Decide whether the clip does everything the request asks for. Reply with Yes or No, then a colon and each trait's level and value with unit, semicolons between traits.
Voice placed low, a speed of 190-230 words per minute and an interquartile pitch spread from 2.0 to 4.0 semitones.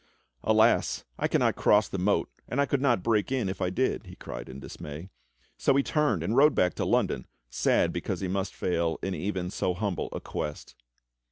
No: very low, 95 Hz; average, 200 wpm; average, 4.7 semitones